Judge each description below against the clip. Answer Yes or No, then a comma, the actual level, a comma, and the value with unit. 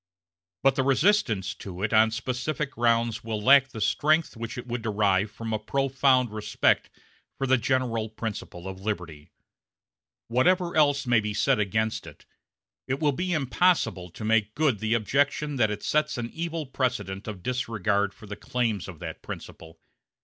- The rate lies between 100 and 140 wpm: No, average, 165 wpm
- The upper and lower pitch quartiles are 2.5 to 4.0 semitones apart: No, average, 4.4 semitones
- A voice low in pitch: Yes, low, 115 Hz